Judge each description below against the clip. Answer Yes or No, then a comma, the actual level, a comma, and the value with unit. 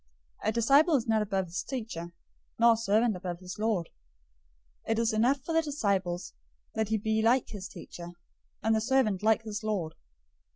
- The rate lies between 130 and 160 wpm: No, average, 190 wpm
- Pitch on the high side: Yes, high, 220 Hz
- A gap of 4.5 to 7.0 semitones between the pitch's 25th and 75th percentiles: No, average, 3.3 semitones